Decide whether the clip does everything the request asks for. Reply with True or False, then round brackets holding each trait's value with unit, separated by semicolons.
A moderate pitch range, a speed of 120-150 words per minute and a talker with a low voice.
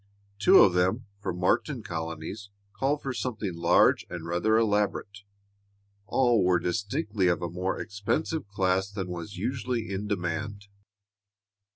True (3.6 semitones; 135 wpm; 100 Hz)